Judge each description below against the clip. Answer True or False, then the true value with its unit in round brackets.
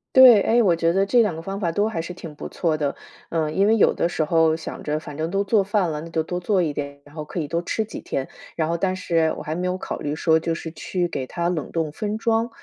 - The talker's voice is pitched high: False (170 Hz)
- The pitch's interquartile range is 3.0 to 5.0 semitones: True (3.8 semitones)